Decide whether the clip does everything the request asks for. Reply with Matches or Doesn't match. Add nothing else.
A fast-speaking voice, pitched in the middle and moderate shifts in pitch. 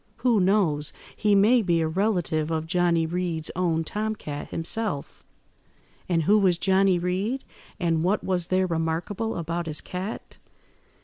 Doesn't match